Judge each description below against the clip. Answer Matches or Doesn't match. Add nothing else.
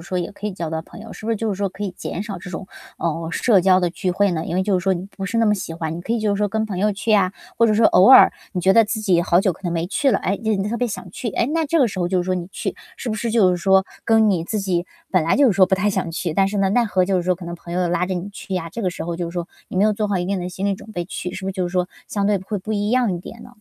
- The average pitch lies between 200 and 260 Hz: Doesn't match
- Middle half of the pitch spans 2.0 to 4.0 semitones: Matches